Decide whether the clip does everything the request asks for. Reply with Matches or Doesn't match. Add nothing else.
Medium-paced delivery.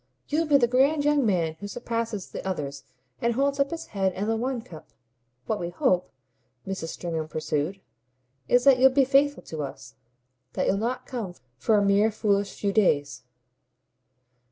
Matches